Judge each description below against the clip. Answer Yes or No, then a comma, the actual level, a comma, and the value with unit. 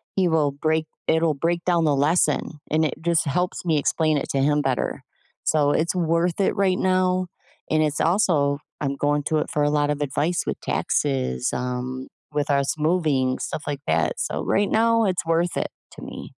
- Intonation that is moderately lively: Yes, average, 3.3 semitones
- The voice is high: No, medium, 155 Hz